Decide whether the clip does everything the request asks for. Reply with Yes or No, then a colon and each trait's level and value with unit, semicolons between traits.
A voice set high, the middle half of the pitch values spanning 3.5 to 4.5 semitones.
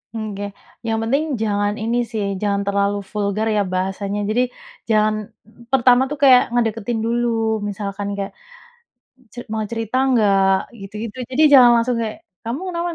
No: high, 220 Hz; average, 2.9 semitones